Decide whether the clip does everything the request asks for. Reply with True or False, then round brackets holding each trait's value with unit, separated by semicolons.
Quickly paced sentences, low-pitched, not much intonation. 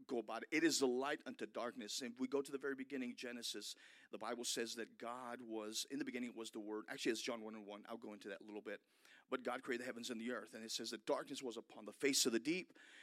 False (295 wpm; 120 Hz; 3.1 semitones)